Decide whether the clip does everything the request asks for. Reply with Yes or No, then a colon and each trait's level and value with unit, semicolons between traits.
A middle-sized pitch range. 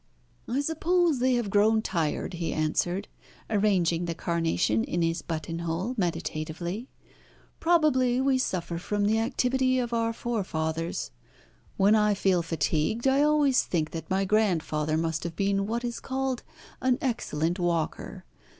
No: wide, 6.8 semitones